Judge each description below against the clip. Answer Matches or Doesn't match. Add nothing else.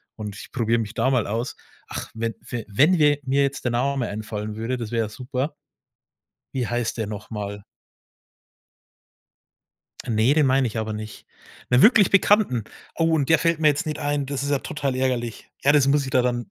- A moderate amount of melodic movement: Matches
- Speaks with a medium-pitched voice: Doesn't match